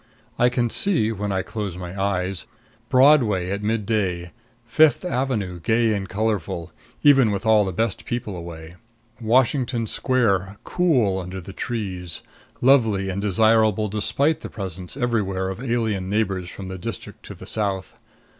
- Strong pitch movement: No, average, 3.7 semitones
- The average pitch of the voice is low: Yes, low, 105 Hz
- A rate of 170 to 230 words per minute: No, average, 145 wpm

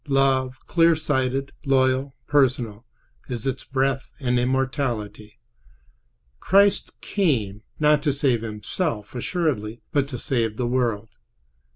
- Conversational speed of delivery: No, slow, 110 wpm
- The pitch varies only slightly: No, average, 3.2 semitones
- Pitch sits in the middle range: No, low, 130 Hz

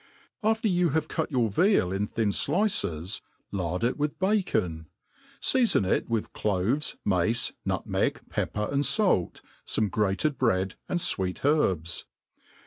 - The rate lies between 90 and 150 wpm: Yes, slow, 135 wpm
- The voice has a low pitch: Yes, low, 115 Hz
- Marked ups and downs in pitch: Yes, wide, 9.0 semitones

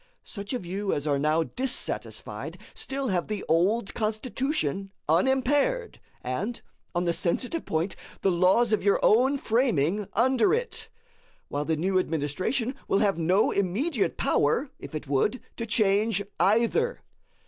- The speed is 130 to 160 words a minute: Yes, average, 140 wpm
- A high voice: Yes, high, 205 Hz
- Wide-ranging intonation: Yes, wide, 6.5 semitones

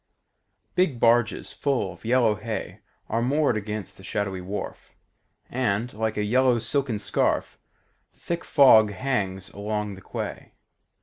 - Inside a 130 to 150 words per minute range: Yes, slow, 135 wpm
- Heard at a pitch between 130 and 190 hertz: No, low, 110 Hz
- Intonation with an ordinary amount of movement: Yes, average, 3.7 semitones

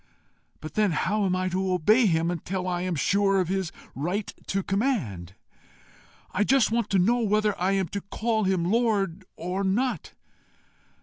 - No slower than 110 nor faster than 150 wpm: No, average, 170 wpm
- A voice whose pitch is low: No, high, 195 Hz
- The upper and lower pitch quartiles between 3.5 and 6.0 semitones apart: No, average, 2.9 semitones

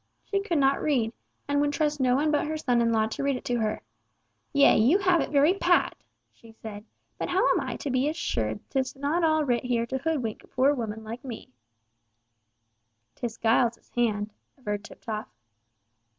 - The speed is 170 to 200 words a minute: Yes, average, 190 wpm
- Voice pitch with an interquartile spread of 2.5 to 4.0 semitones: No, average, 4.7 semitones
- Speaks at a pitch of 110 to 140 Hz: No, very high, 260 Hz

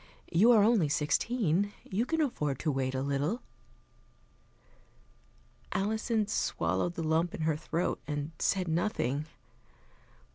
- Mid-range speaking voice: Yes, medium, 170 Hz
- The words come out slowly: Yes, slow, 120 wpm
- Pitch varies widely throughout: Yes, wide, 6.2 semitones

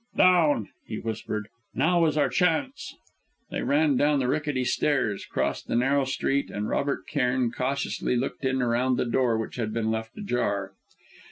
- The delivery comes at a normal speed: Yes, average, 165 wpm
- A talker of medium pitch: No, low, 130 Hz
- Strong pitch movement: No, average, 4.0 semitones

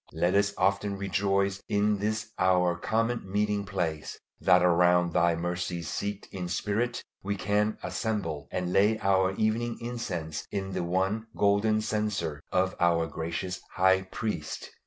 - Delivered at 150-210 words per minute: No, average, 140 wpm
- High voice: No, very low, 95 Hz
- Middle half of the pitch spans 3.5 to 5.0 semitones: No, average, 2.9 semitones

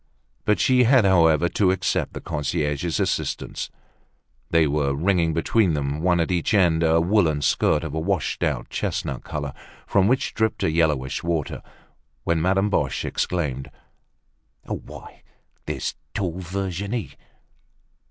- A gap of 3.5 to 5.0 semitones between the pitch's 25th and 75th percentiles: Yes, average, 3.9 semitones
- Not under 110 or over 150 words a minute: Yes, slow, 135 wpm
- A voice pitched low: Yes, very low, 85 Hz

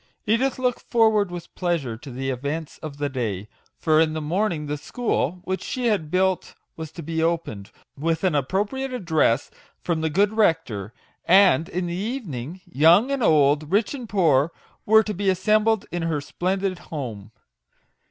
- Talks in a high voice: No, medium, 170 Hz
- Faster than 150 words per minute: Yes, average, 170 wpm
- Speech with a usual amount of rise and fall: No, wide, 5.7 semitones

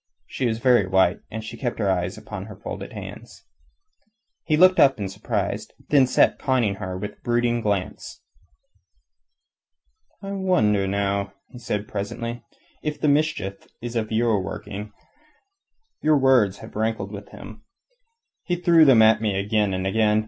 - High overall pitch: No, low, 110 Hz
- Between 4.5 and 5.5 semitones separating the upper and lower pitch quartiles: No, average, 3.8 semitones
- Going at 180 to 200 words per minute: No, average, 155 wpm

